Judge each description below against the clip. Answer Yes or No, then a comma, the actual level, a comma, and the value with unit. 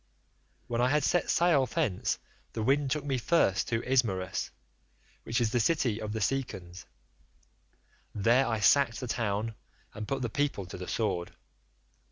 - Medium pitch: No, low, 115 Hz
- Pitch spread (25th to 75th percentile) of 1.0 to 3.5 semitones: No, average, 4.5 semitones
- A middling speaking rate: Yes, average, 160 wpm